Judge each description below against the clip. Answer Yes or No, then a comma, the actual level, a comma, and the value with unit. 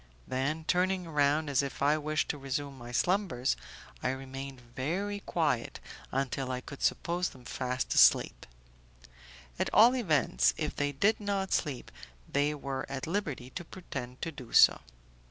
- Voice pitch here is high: No, medium, 145 Hz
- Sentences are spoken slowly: No, average, 155 wpm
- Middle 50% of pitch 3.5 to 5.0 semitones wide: Yes, average, 4.6 semitones